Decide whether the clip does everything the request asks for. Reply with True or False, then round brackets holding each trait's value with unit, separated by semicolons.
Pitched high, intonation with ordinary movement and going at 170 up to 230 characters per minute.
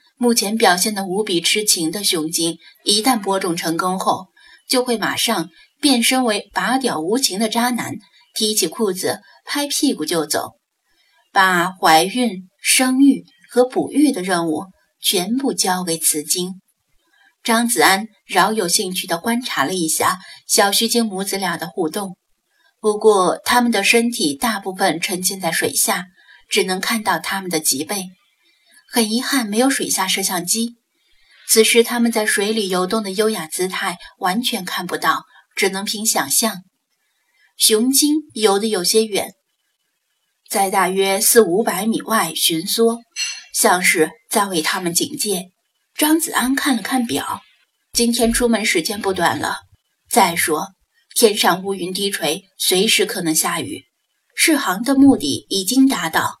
True (215 Hz; 4.6 semitones; 215 characters per minute)